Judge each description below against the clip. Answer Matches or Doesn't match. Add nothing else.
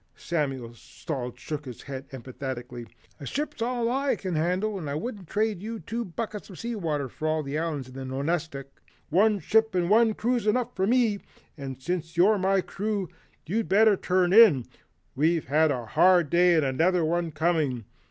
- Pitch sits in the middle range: Matches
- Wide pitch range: Matches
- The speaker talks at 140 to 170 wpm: Doesn't match